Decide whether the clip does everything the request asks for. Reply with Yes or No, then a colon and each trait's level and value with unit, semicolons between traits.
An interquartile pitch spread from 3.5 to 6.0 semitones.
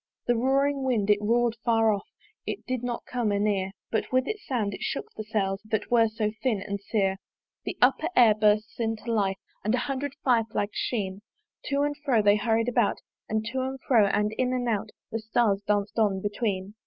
No: average, 3.1 semitones